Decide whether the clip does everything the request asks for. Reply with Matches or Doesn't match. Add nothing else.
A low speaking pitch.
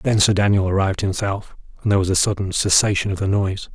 Matches